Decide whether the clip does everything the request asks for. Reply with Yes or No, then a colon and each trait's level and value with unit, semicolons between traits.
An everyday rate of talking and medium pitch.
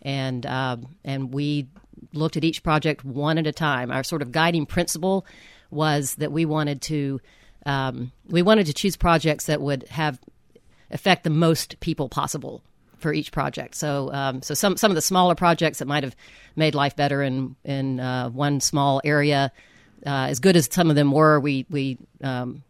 Yes: average, 190 wpm; medium, 145 Hz